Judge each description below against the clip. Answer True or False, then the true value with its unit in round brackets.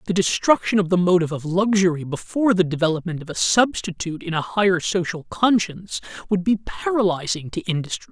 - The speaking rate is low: False (170 wpm)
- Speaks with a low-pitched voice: False (185 Hz)